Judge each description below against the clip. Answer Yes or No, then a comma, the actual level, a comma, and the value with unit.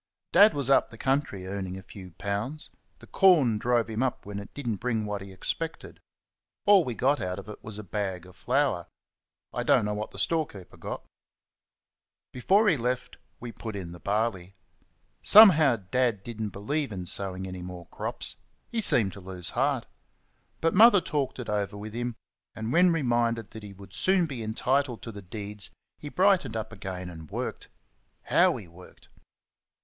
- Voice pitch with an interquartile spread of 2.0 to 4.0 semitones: No, wide, 5.6 semitones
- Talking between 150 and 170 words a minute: No, average, 185 wpm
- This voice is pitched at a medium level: No, low, 110 Hz